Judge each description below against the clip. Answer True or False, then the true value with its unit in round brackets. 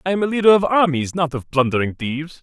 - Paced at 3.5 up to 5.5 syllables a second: False (6.5 syllables/s)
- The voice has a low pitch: False (160 Hz)